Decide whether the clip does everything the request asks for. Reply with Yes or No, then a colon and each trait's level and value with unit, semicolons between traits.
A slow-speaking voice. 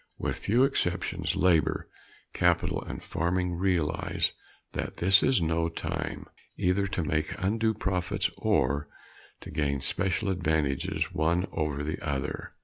Yes: slow, 130 wpm